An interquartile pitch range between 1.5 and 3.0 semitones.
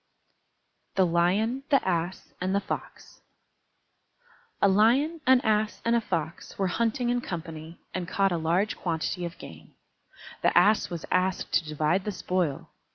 No: average, 4.2 semitones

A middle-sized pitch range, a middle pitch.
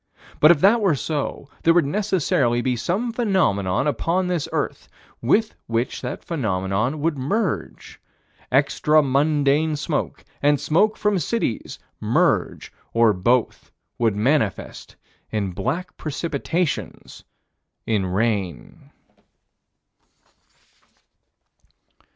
No: wide, 6.7 semitones; medium, 145 Hz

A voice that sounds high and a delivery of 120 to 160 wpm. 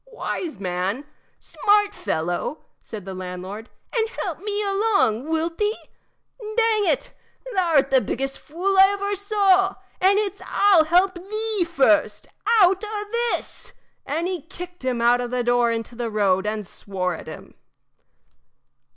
Yes: very high, 335 Hz; average, 150 wpm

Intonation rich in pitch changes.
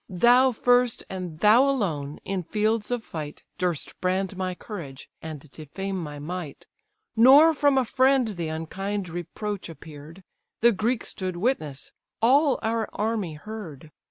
Yes: wide, 6.0 semitones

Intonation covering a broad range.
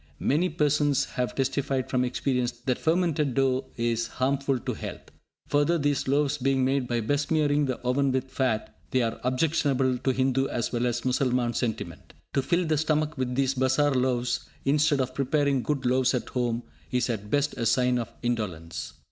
No: narrow, 2.5 semitones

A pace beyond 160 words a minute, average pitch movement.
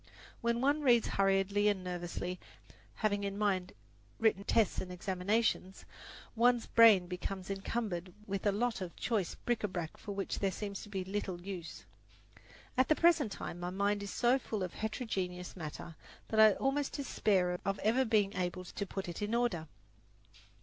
Yes: average, 170 wpm; average, 3.5 semitones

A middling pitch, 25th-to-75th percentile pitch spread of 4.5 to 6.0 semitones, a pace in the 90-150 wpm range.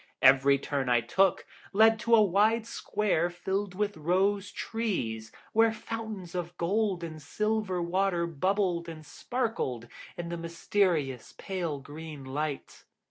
Yes: medium, 175 Hz; average, 5.0 semitones; slow, 135 wpm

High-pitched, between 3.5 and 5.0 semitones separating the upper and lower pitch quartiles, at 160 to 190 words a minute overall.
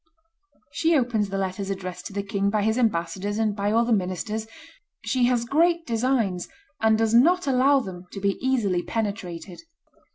Yes: high, 215 Hz; average, 3.8 semitones; average, 170 wpm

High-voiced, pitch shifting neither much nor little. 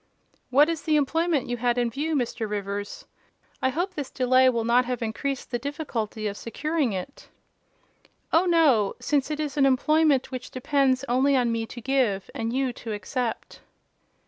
Yes: very high, 255 Hz; average, 3.9 semitones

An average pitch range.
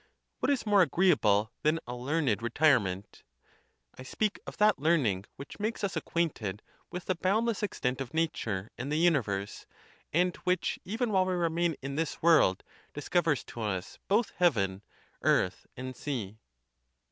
No: wide, 8.0 semitones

